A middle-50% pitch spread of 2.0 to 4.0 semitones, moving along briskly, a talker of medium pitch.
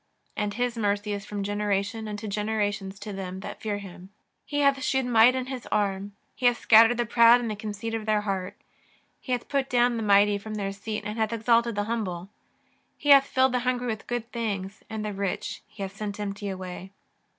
No: average, 2.8 semitones; fast, 210 wpm; high, 215 Hz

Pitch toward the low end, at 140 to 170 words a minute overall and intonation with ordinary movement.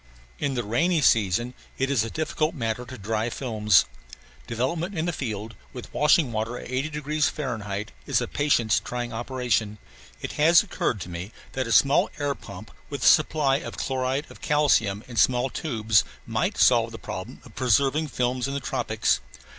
No: low, 125 Hz; average, 180 wpm; average, 4.4 semitones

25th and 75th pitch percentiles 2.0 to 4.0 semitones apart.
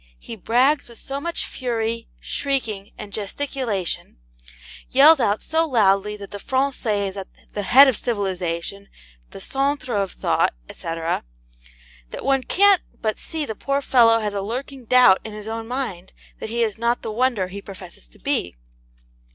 No: average, 4.9 semitones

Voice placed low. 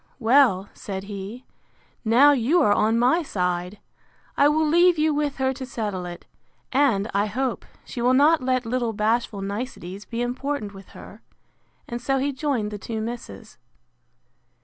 No: high, 240 Hz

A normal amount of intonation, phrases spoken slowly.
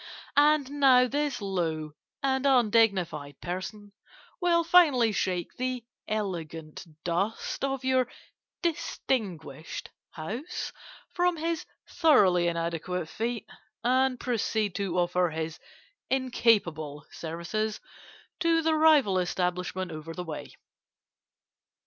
No: wide, 7.4 semitones; slow, 100 wpm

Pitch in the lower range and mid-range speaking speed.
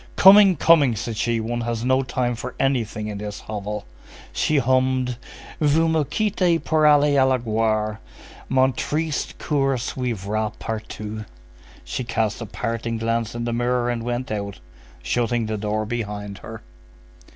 Yes: low, 120 Hz; average, 150 wpm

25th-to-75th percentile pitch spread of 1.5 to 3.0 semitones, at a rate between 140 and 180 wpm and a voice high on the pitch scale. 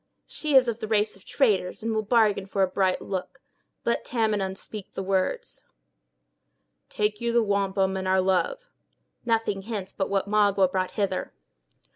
Yes: narrow, 2.6 semitones; average, 165 wpm; high, 200 Hz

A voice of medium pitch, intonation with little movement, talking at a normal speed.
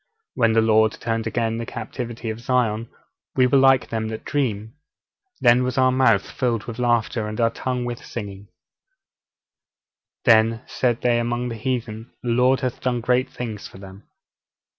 No: low, 115 Hz; narrow, 2.1 semitones; average, 165 wpm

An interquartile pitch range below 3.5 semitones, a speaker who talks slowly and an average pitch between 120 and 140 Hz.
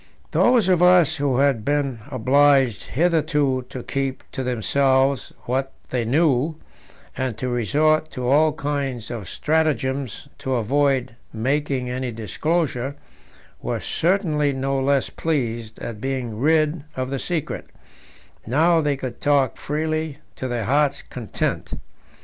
Yes: average, 3.0 semitones; slow, 130 wpm; low, 135 Hz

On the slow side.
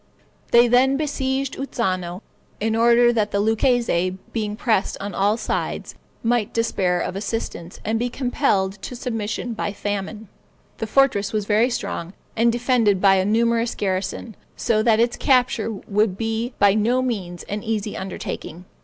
No: average, 155 wpm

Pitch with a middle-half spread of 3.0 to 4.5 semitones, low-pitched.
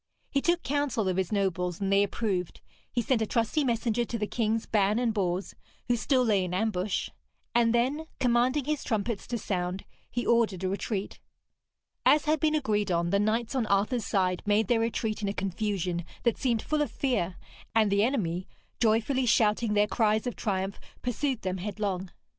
No: average, 3.7 semitones; high, 215 Hz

